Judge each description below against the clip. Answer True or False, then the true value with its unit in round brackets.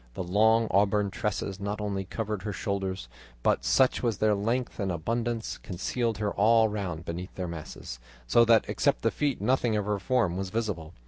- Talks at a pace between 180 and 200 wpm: True (185 wpm)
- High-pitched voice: False (105 Hz)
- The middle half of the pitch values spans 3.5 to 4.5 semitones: False (3.1 semitones)